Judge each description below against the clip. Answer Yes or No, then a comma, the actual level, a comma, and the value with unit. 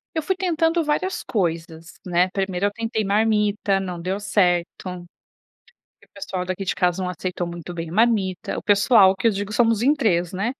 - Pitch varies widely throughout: No, average, 3.8 semitones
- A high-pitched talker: Yes, high, 195 Hz